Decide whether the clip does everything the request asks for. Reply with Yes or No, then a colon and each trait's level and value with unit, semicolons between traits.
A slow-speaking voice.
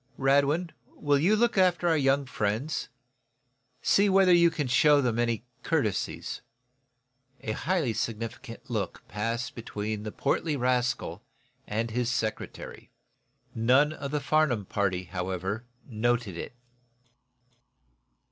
Yes: slow, 120 wpm